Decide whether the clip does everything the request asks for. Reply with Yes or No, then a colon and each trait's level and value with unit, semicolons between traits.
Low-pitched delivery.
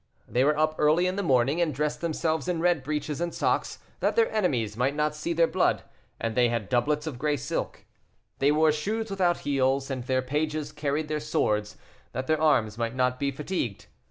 No: medium, 150 Hz